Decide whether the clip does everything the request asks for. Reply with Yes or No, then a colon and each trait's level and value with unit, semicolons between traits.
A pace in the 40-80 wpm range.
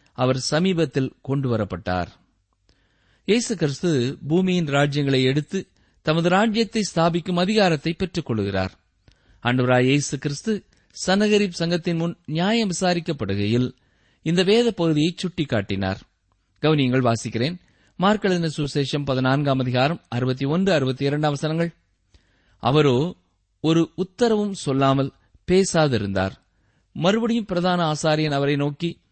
Yes: slow, 75 wpm